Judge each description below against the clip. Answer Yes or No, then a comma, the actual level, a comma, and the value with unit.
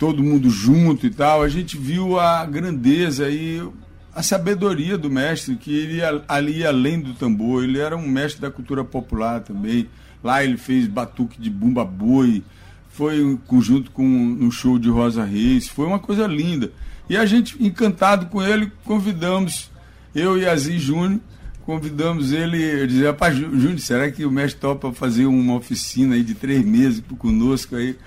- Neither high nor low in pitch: Yes, medium, 145 Hz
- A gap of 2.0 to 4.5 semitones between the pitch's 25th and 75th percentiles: No, wide, 5.5 semitones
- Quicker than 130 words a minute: Yes, average, 175 wpm